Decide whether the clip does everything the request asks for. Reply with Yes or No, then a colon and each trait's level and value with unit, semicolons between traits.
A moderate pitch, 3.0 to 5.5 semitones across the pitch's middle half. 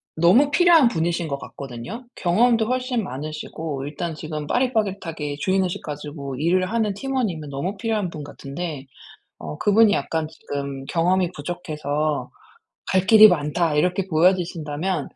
Yes: medium, 170 Hz; average, 5.1 semitones